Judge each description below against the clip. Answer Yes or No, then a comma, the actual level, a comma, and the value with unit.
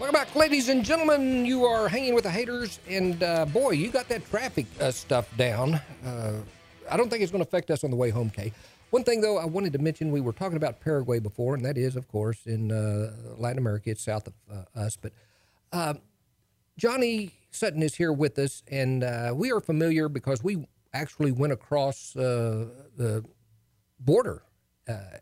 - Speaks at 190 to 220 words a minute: Yes, average, 200 wpm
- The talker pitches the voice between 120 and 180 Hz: Yes, medium, 140 Hz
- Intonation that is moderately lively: No, wide, 8.6 semitones